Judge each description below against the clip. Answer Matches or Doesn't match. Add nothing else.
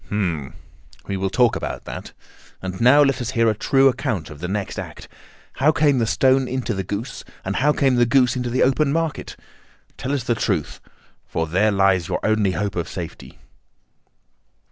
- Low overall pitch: Matches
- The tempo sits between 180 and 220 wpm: Matches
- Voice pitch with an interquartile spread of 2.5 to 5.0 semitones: Doesn't match